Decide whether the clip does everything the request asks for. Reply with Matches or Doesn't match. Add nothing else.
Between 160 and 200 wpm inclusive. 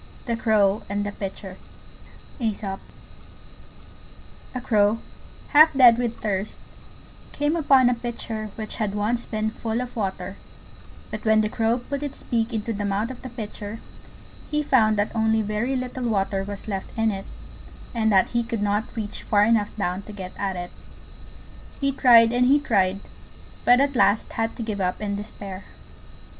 Matches